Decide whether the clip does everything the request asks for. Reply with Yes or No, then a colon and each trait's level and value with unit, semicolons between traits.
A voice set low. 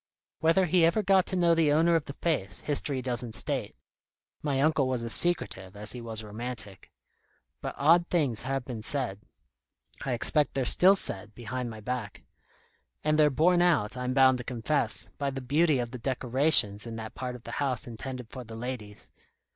Yes: low, 130 Hz